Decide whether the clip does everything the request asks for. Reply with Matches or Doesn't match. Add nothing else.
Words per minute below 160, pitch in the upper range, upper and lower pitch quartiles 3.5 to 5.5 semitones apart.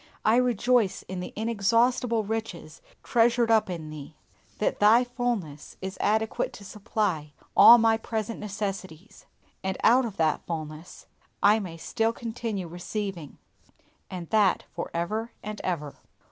Matches